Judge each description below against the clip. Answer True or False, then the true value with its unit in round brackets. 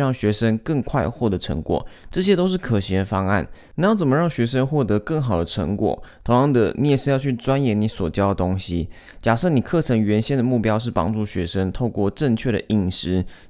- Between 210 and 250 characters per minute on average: False (310 characters per minute)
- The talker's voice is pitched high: False (110 Hz)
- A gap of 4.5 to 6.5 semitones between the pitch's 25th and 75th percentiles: True (5.2 semitones)